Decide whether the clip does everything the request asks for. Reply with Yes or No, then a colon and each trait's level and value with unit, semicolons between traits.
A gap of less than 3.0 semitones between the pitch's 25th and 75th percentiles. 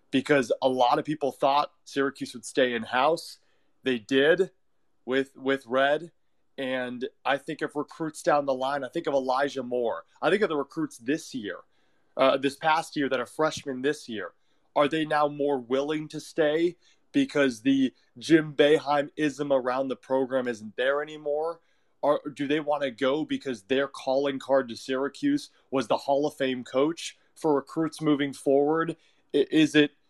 Yes: narrow, 2.5 semitones